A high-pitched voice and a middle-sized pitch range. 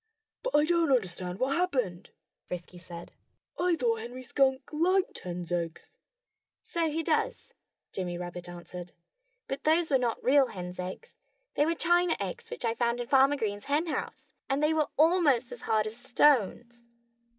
No: very high, 255 Hz; wide, 8.6 semitones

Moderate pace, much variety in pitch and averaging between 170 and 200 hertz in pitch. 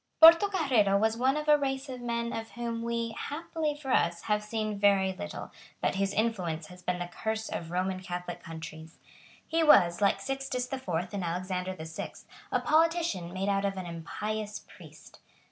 No: average, 180 wpm; wide, 5.9 semitones; high, 210 Hz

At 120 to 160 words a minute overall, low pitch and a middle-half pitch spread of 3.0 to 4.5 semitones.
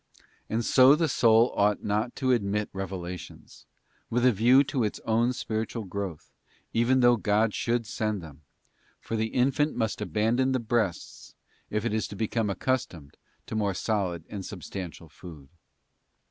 Yes: average, 155 wpm; low, 110 Hz; average, 3.5 semitones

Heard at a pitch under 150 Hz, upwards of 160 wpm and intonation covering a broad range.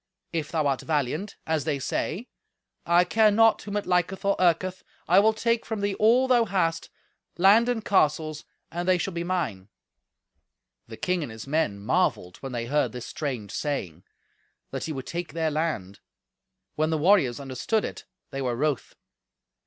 No: medium, 165 Hz; average, 175 wpm; wide, 6.1 semitones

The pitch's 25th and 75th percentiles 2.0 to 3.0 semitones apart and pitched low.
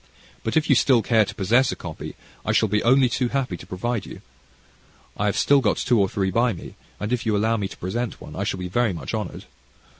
No: average, 3.9 semitones; low, 110 Hz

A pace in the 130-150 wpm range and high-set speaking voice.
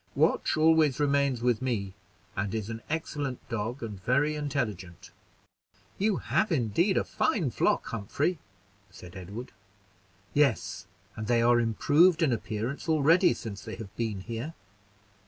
No: slow, 135 wpm; low, 125 Hz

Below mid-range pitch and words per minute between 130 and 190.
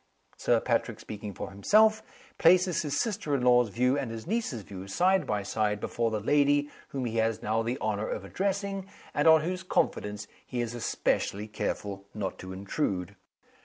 Yes: low, 120 Hz; average, 175 wpm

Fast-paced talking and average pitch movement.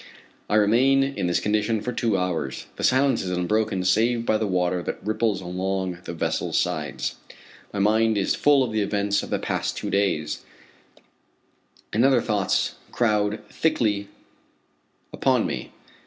No: average, 155 wpm; average, 3.3 semitones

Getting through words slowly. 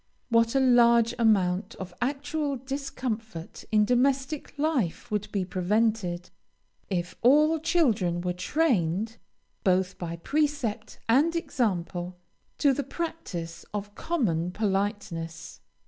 Yes: slow, 110 wpm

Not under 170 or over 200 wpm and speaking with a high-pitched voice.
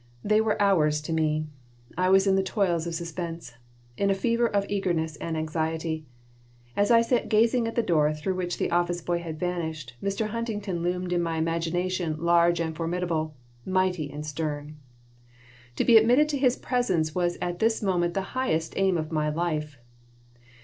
No: average, 175 wpm; medium, 175 Hz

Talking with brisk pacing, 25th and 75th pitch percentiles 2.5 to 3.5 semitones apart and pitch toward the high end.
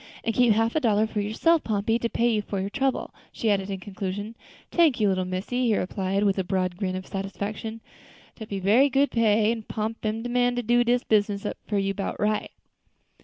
Yes: fast, 220 wpm; average, 2.9 semitones; high, 215 Hz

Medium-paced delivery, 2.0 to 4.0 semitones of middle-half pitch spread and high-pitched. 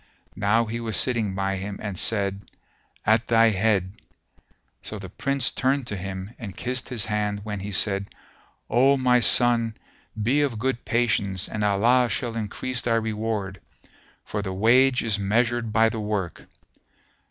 No: average, 155 wpm; average, 3.1 semitones; low, 110 Hz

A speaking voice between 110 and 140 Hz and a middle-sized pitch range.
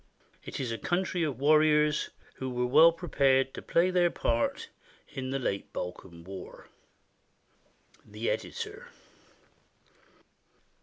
Yes: low, 135 Hz; average, 4.9 semitones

